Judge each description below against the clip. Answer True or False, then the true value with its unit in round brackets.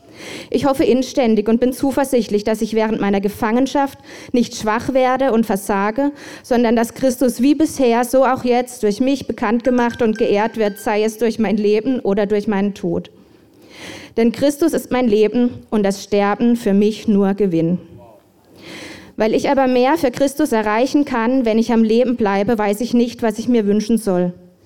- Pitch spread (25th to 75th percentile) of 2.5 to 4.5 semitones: True (3.4 semitones)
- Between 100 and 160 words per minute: False (180 wpm)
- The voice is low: False (230 Hz)